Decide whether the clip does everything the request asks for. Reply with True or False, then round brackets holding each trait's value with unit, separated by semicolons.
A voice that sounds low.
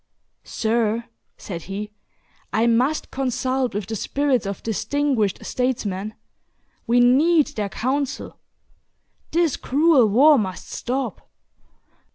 False (245 Hz)